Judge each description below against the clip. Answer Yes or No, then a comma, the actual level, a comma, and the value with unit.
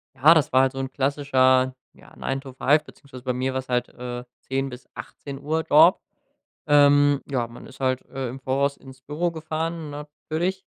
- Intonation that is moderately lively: No, narrow, 2.3 semitones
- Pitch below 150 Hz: Yes, low, 135 Hz